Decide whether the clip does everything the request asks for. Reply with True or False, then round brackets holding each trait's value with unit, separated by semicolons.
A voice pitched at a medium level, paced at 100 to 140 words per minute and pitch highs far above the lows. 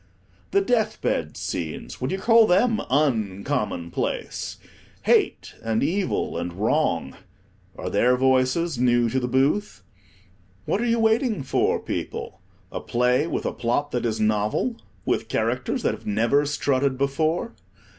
False (130 Hz; 135 wpm; 7.4 semitones)